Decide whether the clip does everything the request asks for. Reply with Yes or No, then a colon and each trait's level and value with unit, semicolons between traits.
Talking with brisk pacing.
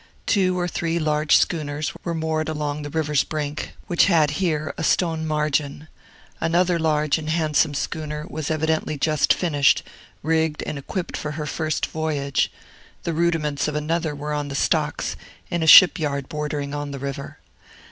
No: average, 160 wpm